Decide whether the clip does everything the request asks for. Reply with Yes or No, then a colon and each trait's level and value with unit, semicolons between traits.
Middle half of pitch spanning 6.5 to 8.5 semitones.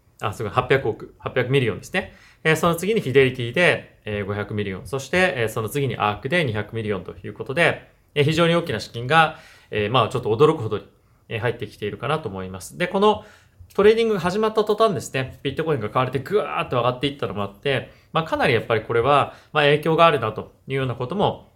Yes: wide, 6.9 semitones